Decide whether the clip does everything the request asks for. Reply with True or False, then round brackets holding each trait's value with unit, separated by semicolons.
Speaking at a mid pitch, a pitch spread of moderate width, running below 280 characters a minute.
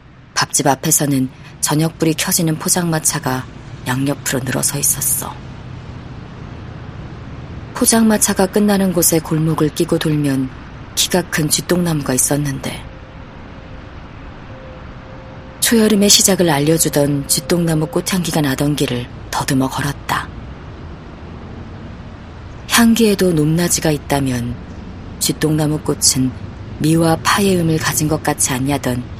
True (145 Hz; 4.5 semitones; 240 characters per minute)